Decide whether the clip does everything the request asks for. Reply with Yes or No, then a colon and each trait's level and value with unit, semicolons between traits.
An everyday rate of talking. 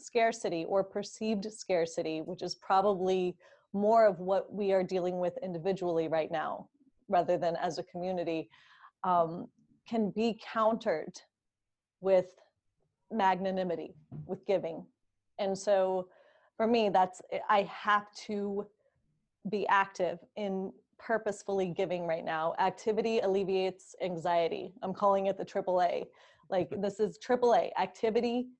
No: slow, 120 wpm